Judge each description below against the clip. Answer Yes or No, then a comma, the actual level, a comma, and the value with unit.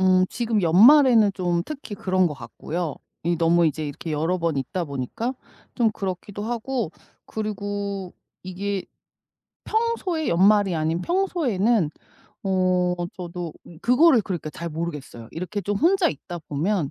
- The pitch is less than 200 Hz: Yes, medium, 185 Hz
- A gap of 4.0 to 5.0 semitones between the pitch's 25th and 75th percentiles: Yes, average, 4.6 semitones